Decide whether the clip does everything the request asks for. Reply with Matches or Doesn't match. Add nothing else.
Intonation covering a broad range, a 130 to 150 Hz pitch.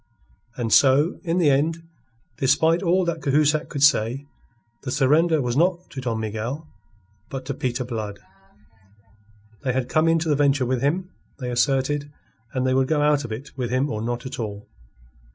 Doesn't match